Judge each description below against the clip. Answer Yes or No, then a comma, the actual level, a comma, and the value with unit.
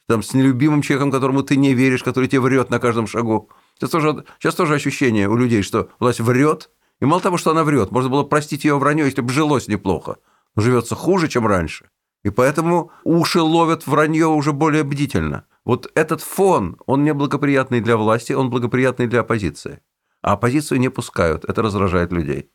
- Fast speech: Yes, fast, 185 wpm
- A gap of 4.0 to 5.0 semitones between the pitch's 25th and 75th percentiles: Yes, average, 4.7 semitones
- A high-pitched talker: No, low, 135 Hz